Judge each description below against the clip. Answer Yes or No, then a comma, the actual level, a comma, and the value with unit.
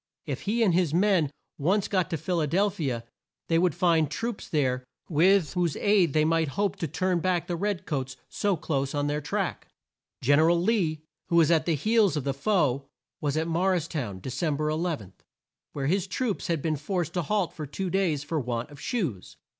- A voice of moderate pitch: Yes, medium, 165 Hz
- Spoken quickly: Yes, fast, 215 wpm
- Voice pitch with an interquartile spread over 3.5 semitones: Yes, average, 4.1 semitones